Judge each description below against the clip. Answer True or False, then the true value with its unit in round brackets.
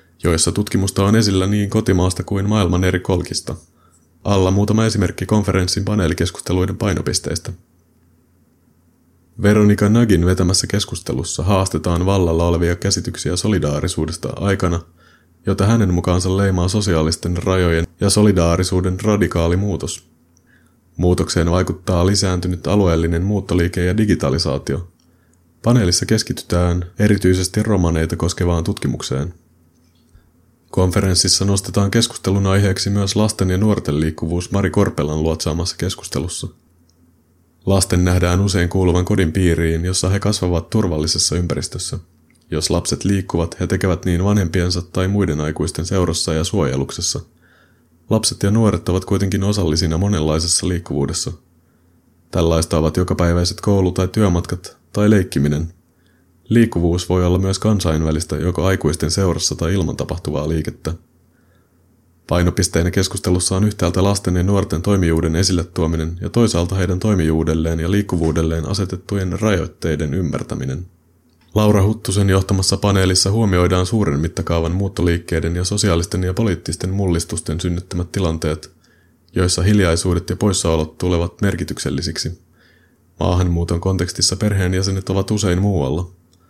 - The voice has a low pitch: True (90 Hz)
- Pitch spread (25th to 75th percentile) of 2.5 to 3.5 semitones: True (2.9 semitones)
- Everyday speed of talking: True (110 wpm)